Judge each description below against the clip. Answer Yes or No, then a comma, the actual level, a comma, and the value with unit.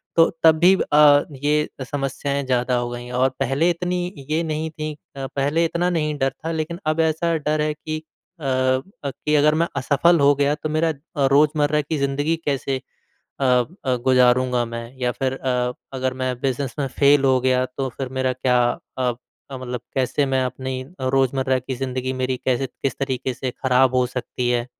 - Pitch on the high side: No, low, 135 Hz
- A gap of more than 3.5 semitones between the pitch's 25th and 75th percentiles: No, average, 2.9 semitones